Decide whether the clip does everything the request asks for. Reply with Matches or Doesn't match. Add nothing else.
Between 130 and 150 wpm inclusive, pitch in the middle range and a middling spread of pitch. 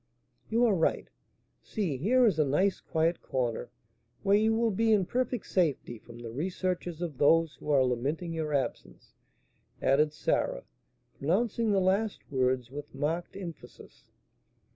Doesn't match